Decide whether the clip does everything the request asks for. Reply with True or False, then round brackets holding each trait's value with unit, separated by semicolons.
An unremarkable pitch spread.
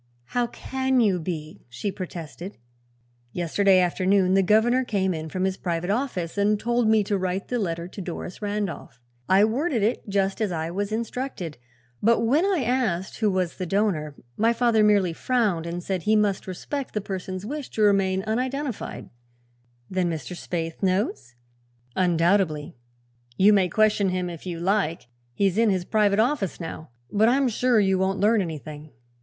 True (3.7 semitones)